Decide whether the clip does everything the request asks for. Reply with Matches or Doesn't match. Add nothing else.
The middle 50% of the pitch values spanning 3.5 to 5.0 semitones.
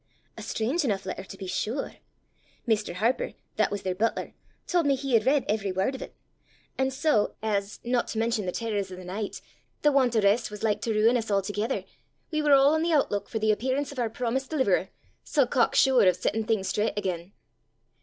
Matches